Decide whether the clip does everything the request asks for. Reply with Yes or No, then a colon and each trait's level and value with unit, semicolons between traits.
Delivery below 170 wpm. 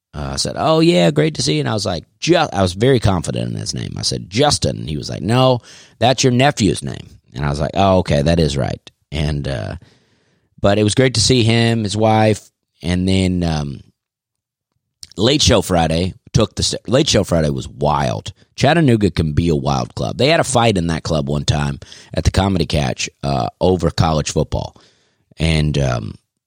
No: fast, 205 wpm